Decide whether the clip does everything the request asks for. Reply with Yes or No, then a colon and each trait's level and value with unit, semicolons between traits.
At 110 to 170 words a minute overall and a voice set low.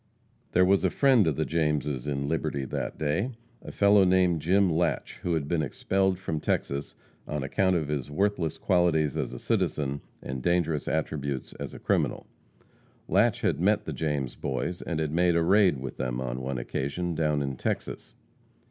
No: average, 180 wpm; very low, 80 Hz